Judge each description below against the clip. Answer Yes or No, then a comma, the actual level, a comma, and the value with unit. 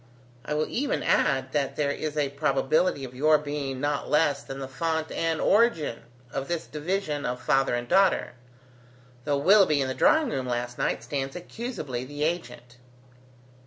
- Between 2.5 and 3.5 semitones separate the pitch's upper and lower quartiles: Yes, average, 3.2 semitones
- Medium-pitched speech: Yes, medium, 145 Hz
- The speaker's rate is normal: Yes, average, 160 wpm